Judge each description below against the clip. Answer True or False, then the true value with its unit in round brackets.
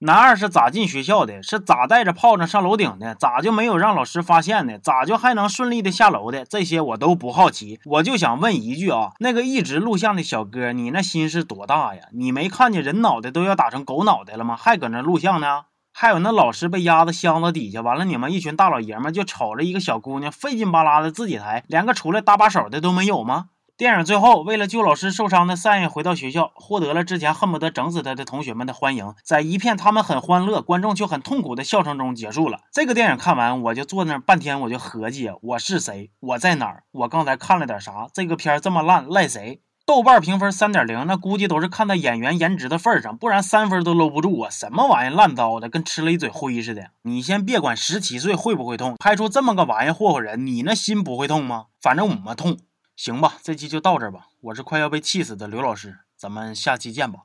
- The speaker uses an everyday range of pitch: False (6.8 semitones)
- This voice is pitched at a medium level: True (175 Hz)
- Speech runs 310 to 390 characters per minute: True (360 characters per minute)